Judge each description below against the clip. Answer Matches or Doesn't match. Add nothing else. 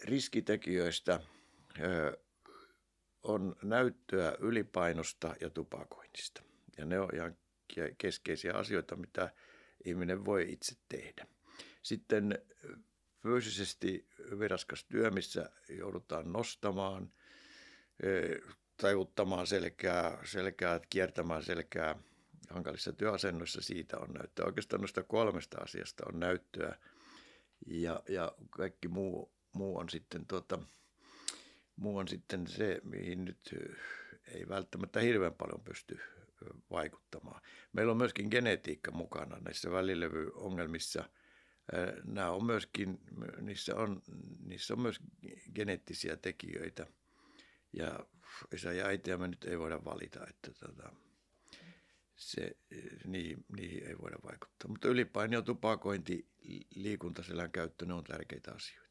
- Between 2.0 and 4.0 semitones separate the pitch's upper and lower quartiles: Matches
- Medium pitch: Doesn't match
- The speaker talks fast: Doesn't match